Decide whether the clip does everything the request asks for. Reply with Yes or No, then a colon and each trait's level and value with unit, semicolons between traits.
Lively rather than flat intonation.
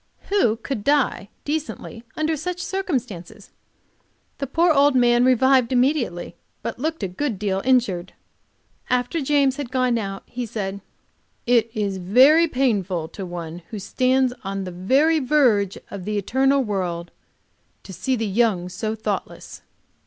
Yes: wide, 5.7 semitones